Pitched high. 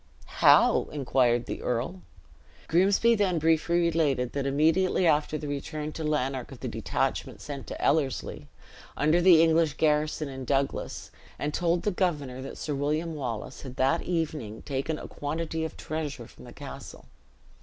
No: medium, 150 Hz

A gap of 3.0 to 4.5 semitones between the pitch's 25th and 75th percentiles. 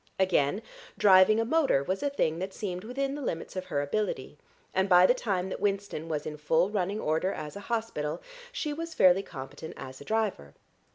No: wide, 5.4 semitones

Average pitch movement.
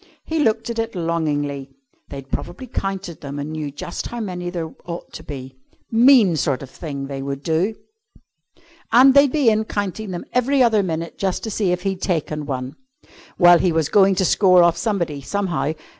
No: wide, 6.3 semitones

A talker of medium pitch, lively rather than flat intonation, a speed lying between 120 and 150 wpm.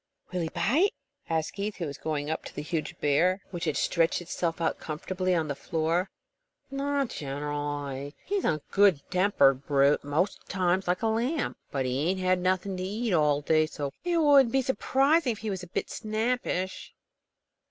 No: medium, 180 Hz; wide, 6.1 semitones; average, 175 wpm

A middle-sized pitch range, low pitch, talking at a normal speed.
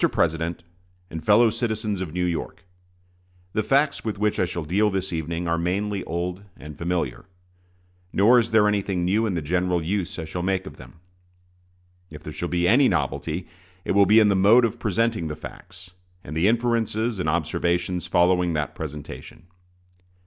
Yes: average, 3.8 semitones; very low, 90 Hz; average, 175 wpm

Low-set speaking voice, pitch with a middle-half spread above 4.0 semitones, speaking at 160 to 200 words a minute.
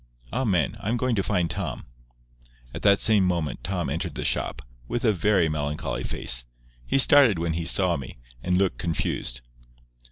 Yes: very low, 90 Hz; average, 4.6 semitones; average, 165 wpm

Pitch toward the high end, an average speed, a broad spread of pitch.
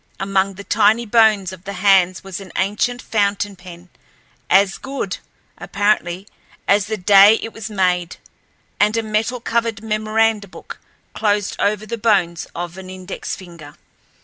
No: high, 200 Hz; average, 150 wpm; narrow, 2.5 semitones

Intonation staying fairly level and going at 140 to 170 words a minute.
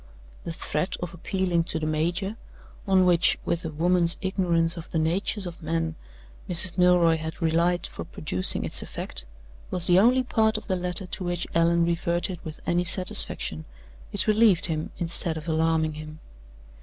Yes: narrow, 2.1 semitones; average, 165 wpm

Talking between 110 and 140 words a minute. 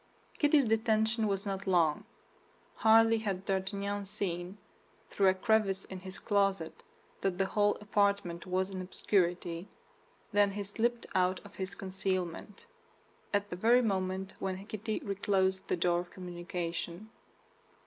Yes: slow, 135 wpm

